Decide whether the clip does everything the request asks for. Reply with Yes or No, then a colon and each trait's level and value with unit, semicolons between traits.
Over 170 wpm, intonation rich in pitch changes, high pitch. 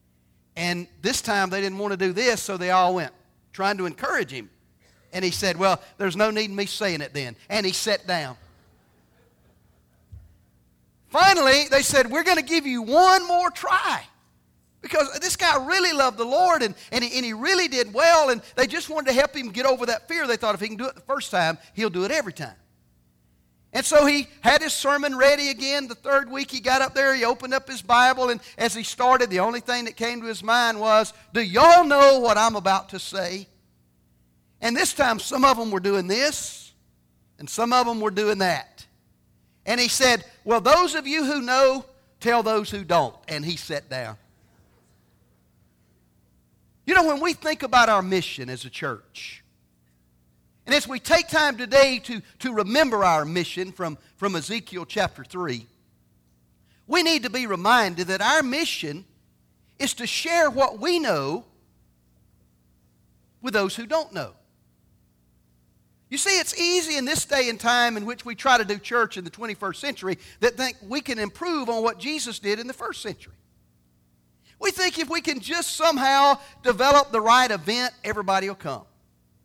Yes: average, 190 wpm; wide, 8.8 semitones; high, 225 Hz